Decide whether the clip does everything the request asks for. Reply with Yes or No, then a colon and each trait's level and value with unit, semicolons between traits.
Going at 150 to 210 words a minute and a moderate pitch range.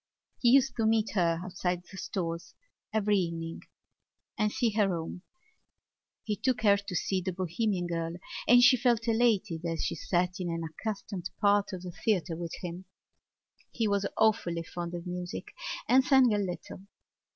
Yes: average, 165 wpm; average, 4.0 semitones